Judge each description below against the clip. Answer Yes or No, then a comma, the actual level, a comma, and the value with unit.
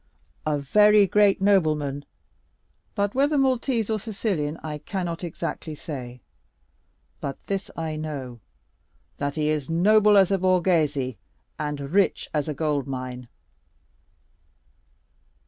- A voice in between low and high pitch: Yes, medium, 160 Hz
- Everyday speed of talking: No, slow, 115 wpm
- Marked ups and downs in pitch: Yes, wide, 5.8 semitones